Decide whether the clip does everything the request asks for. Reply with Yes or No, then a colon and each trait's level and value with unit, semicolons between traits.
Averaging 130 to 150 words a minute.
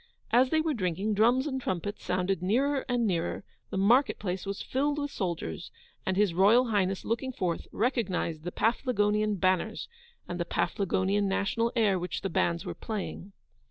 No: average, 160 wpm